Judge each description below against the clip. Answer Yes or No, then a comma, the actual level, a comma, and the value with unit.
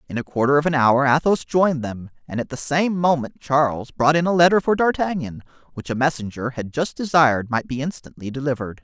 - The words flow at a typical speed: No, fast, 210 wpm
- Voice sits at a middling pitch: Yes, medium, 145 Hz